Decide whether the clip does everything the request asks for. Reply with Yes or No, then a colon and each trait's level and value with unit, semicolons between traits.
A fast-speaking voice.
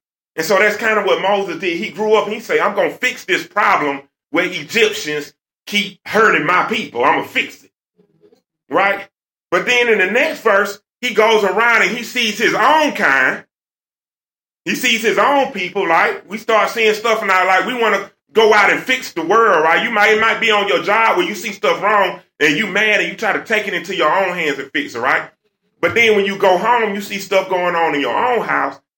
Yes: fast, 235 wpm